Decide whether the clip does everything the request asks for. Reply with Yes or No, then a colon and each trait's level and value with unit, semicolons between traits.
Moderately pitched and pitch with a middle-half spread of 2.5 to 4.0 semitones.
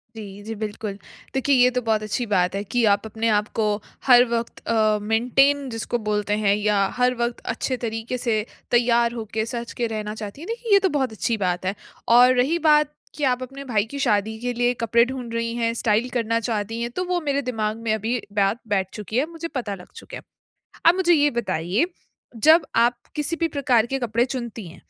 No: high, 235 Hz; average, 3.0 semitones